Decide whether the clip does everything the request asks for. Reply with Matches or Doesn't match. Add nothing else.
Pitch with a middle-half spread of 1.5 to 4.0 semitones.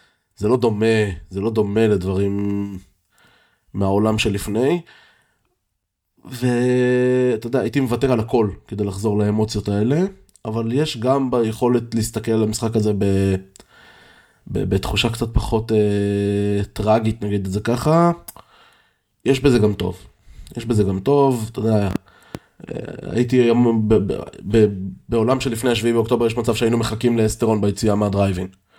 Matches